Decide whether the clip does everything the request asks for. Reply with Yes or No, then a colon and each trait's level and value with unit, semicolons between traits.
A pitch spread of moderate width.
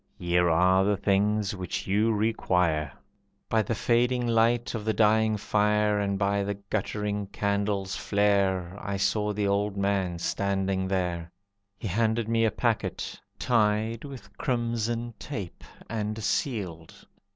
No: narrow, 2.3 semitones